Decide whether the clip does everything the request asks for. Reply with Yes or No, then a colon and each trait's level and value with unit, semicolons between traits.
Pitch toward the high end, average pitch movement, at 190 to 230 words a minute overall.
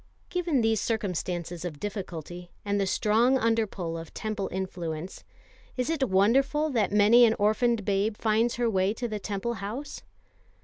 No: high, 210 Hz; average, 3.8 semitones; average, 160 wpm